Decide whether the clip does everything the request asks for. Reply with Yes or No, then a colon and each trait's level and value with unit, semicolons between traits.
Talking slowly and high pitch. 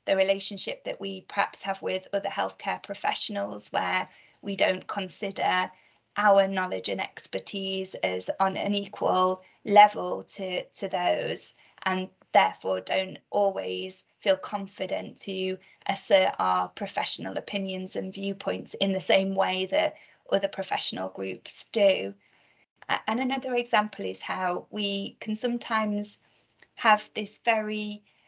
Yes: slow, 125 wpm; high, 195 Hz